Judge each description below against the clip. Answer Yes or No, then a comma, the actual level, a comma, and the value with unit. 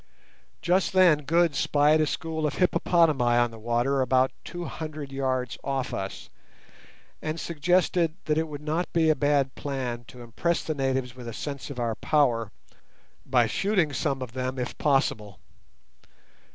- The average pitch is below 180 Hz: Yes, medium, 140 Hz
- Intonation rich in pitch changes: No, average, 3.9 semitones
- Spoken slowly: No, average, 160 wpm